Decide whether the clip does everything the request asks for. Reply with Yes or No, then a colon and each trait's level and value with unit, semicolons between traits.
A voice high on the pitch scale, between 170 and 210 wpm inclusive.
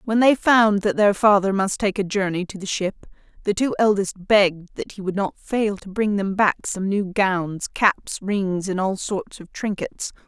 Yes: high, 200 Hz; fast, 205 wpm